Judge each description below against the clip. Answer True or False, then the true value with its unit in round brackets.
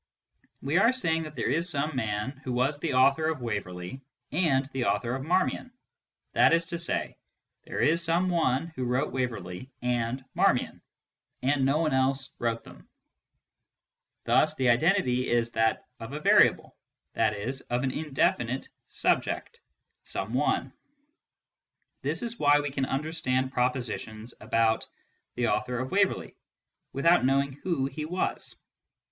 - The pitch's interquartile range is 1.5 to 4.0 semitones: False (4.4 semitones)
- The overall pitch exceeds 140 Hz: False (135 Hz)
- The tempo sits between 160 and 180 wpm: False (150 wpm)